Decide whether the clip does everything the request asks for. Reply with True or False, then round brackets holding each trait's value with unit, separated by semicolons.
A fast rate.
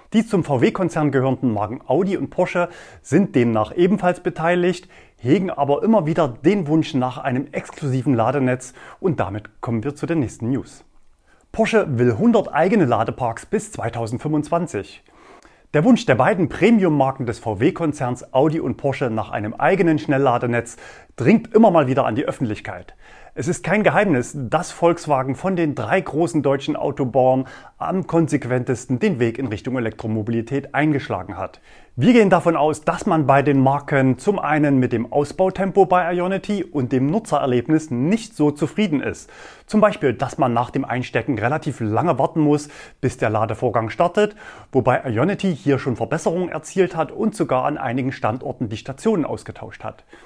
False (160 wpm)